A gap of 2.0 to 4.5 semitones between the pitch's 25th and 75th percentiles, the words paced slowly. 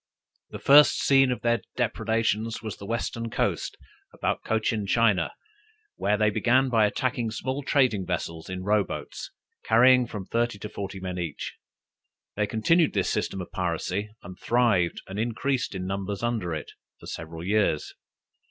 No: average, 3.9 semitones; average, 155 wpm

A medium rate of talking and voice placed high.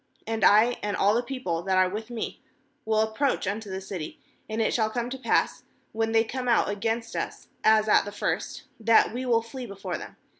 No: fast, 215 wpm; high, 220 Hz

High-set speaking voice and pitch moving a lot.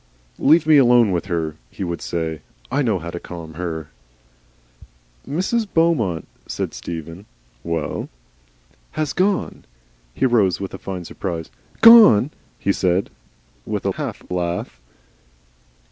No: very low, 95 Hz; wide, 8.6 semitones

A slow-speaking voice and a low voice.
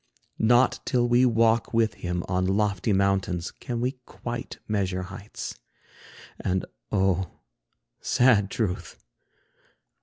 Yes: slow, 110 wpm; low, 100 Hz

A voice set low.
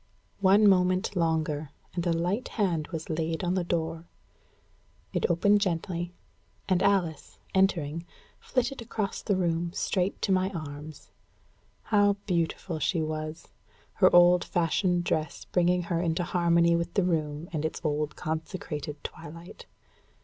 No: medium, 170 Hz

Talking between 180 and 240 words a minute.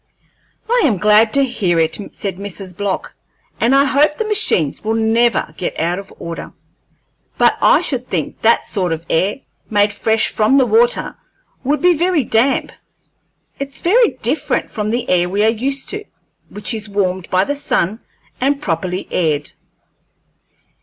No: average, 160 wpm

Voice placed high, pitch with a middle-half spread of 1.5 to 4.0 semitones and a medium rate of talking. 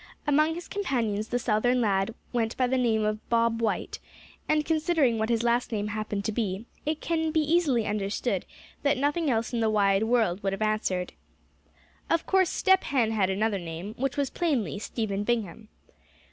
No: high, 230 Hz; average, 5.0 semitones; average, 180 wpm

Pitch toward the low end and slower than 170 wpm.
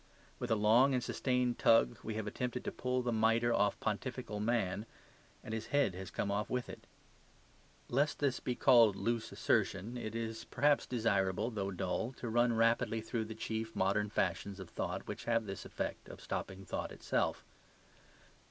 No: low, 115 Hz; average, 180 wpm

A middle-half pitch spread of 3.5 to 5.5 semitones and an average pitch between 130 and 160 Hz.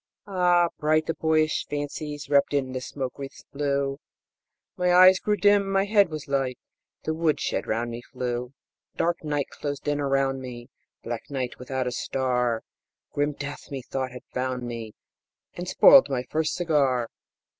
Yes: average, 3.8 semitones; medium, 140 Hz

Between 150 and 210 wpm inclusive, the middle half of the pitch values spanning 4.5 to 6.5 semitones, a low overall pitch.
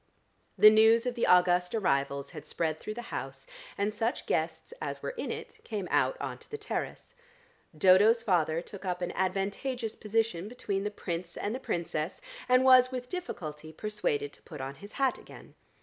No: average, 180 wpm; average, 5.2 semitones; high, 205 Hz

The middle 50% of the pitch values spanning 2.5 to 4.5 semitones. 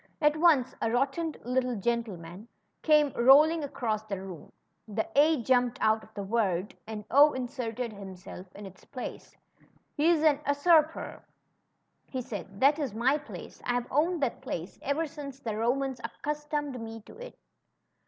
No: average, 5.1 semitones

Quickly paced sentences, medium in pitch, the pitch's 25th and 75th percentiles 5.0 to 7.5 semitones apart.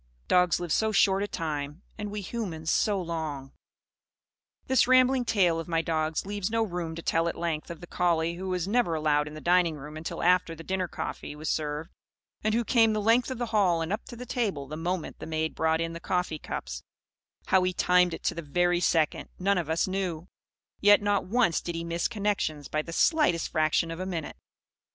No: fast, 215 wpm; medium, 175 Hz; average, 3.9 semitones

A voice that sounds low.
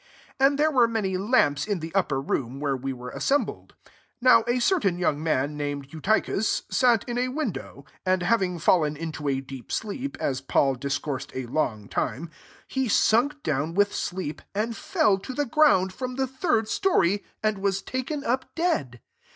No: high, 190 Hz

